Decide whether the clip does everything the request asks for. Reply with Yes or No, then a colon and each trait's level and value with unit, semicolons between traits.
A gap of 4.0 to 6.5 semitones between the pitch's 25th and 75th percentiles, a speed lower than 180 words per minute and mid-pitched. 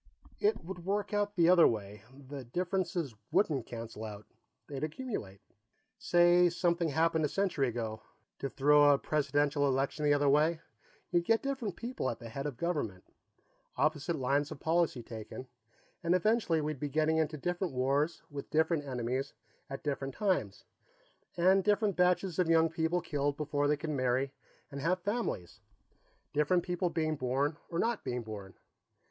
Yes: average, 4.4 semitones; average, 165 wpm; medium, 155 Hz